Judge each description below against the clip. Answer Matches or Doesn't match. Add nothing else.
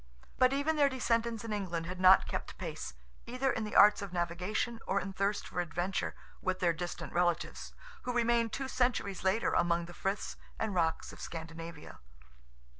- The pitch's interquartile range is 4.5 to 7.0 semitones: Matches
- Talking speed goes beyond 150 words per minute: Matches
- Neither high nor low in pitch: Doesn't match